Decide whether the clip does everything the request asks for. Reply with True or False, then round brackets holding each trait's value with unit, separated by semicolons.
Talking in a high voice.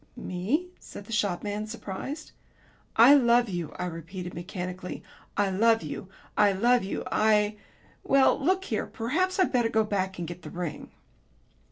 True (210 Hz)